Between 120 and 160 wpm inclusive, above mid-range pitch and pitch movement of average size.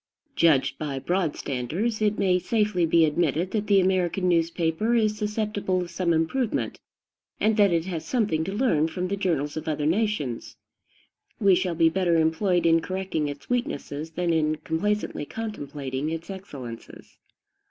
No: average, 155 wpm; medium, 175 Hz; average, 4.3 semitones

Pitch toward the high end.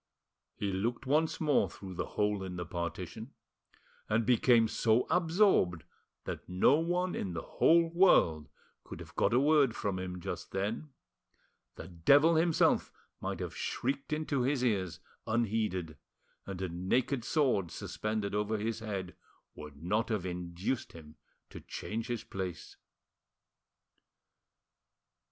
No: low, 110 Hz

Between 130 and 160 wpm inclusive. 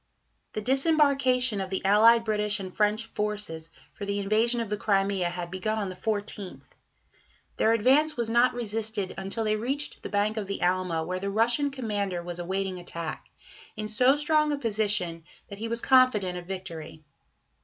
No: average, 175 wpm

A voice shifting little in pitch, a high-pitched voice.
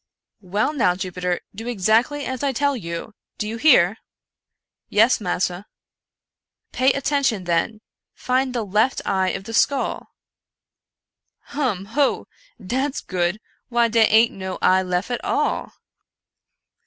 No: wide, 5.6 semitones; high, 220 Hz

